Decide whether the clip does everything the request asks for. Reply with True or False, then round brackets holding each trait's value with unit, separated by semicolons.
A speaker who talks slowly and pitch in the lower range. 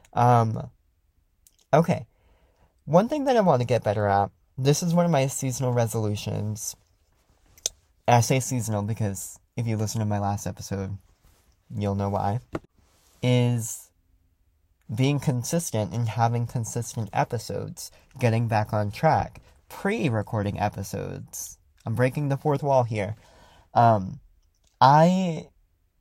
True (125 wpm; 110 Hz)